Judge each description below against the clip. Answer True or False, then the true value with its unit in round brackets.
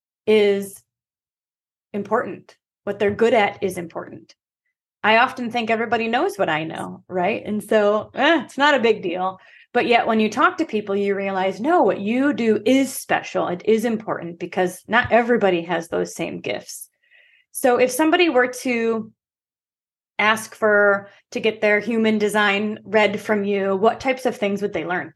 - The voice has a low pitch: False (215 Hz)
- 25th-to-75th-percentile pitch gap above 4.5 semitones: False (3.5 semitones)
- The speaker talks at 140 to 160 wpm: False (170 wpm)